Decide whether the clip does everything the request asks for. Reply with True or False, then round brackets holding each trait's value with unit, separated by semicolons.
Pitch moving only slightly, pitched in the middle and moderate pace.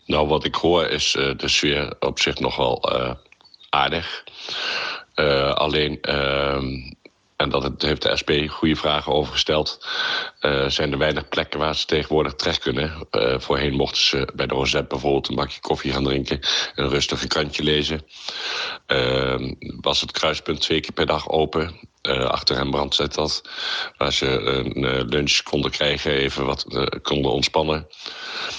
False (2.0 semitones; 70 Hz; 170 wpm)